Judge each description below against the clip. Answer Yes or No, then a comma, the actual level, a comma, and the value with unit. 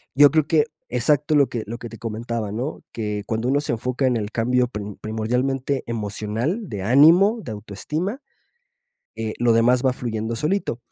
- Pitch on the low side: Yes, low, 120 Hz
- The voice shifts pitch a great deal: No, average, 4.2 semitones